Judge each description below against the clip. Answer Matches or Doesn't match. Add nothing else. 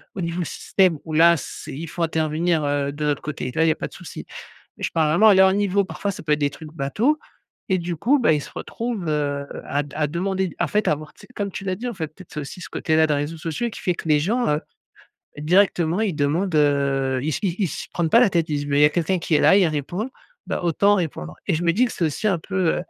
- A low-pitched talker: Doesn't match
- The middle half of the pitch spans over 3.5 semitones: Matches